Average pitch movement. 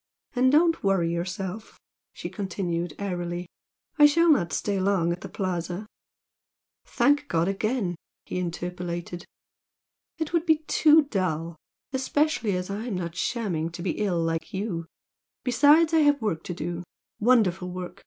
No: wide, 6.5 semitones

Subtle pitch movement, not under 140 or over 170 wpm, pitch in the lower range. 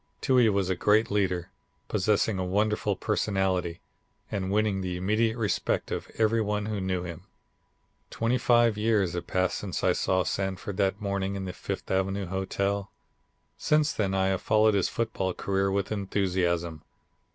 Yes: narrow, 2.2 semitones; average, 160 wpm; low, 100 Hz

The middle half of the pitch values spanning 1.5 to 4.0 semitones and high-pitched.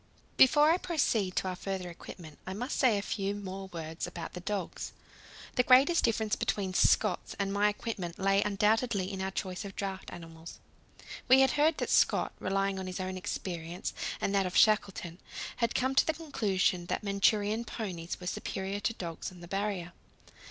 Yes: average, 3.1 semitones; high, 195 Hz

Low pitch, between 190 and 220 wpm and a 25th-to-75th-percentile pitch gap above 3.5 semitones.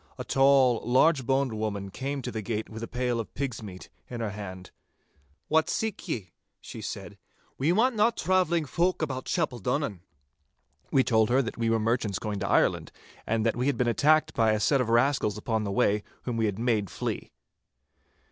Yes: low, 120 Hz; average, 195 wpm; average, 4.4 semitones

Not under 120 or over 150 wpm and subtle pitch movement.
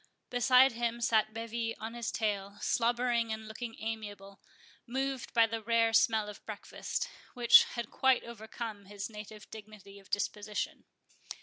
Yes: average, 145 wpm; narrow, 2.0 semitones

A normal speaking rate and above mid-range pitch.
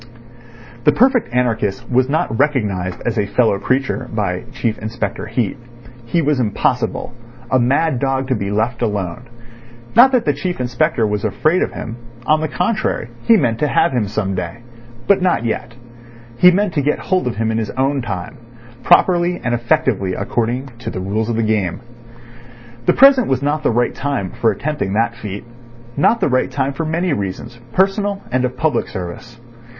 No: average, 180 wpm; low, 125 Hz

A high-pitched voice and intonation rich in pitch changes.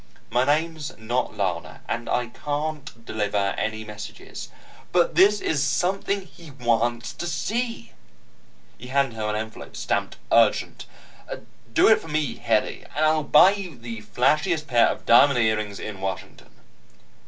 No: low, 125 Hz; wide, 6.0 semitones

